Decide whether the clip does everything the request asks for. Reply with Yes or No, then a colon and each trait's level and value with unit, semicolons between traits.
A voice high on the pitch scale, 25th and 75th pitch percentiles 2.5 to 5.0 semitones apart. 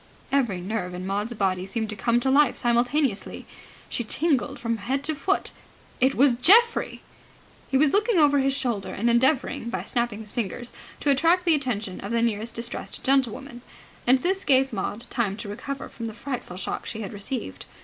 Yes: high, 240 Hz; average, 4.5 semitones